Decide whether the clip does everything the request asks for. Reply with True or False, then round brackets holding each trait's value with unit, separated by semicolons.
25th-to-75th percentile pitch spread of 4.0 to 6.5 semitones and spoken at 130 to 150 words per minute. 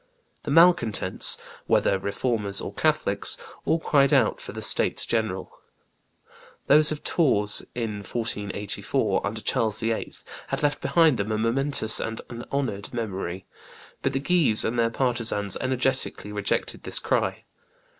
True (4.7 semitones; 135 wpm)